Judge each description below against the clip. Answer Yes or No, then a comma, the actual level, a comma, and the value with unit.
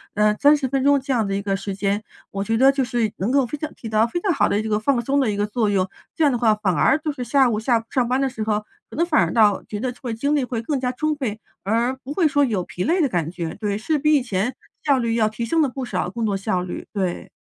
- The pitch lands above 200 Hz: Yes, high, 235 Hz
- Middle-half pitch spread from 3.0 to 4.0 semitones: No, average, 4.8 semitones